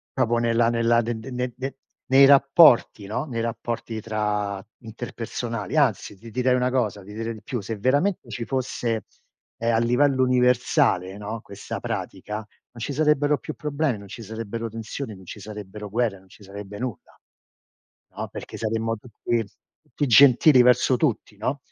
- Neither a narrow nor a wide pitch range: Yes, average, 3.1 semitones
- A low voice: Yes, low, 115 Hz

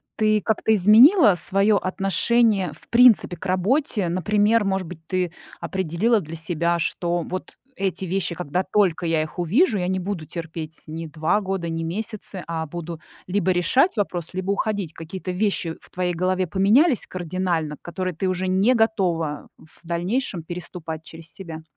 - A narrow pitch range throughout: No, average, 3.5 semitones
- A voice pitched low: No, medium, 185 Hz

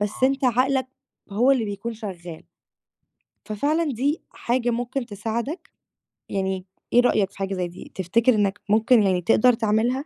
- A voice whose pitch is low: No, high, 225 Hz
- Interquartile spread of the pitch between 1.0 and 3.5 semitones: No, average, 4.2 semitones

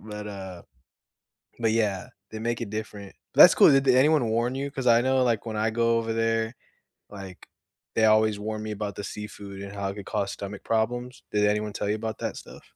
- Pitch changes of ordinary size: No, narrow, 2.1 semitones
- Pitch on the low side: Yes, low, 110 Hz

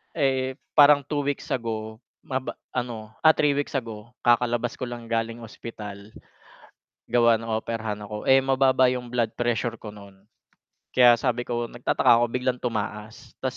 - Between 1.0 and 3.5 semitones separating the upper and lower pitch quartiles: Yes, average, 2.7 semitones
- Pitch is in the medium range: No, low, 120 Hz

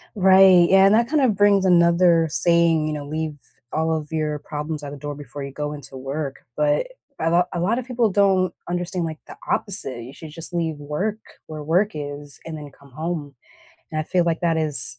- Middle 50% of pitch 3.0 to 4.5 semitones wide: Yes, average, 3.7 semitones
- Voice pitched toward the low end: No, medium, 160 Hz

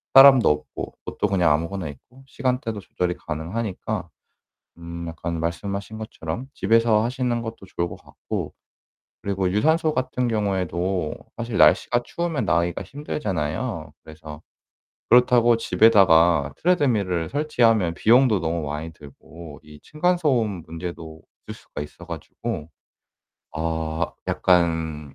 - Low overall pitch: Yes, very low, 95 Hz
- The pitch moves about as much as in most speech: No, wide, 6.4 semitones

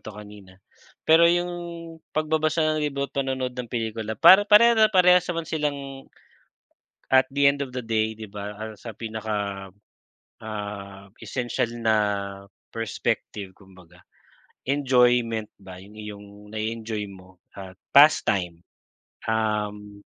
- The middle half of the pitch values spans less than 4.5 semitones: No, average, 5.2 semitones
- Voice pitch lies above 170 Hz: No, low, 110 Hz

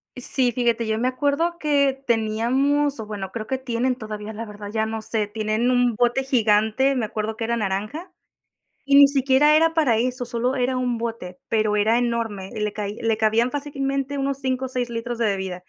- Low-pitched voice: No, high, 235 Hz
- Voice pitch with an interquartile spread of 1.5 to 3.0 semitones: No, average, 3.4 semitones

